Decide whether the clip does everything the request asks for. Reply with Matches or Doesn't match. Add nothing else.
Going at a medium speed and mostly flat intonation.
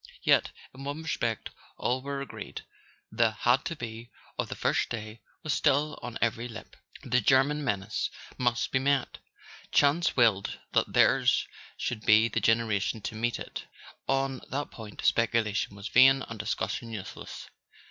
Doesn't match